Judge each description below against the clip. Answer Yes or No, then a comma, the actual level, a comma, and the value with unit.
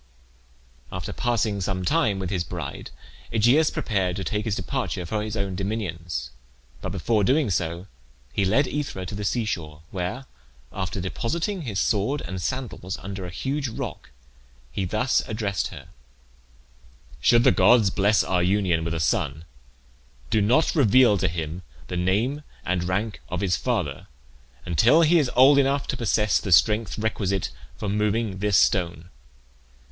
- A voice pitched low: Yes, low, 100 Hz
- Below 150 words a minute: No, average, 155 wpm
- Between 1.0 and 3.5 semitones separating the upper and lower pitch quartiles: No, average, 4.6 semitones